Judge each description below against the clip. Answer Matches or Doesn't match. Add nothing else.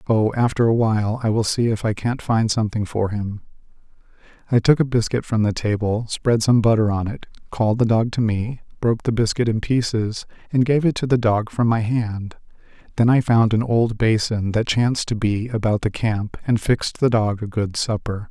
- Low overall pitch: Matches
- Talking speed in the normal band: Doesn't match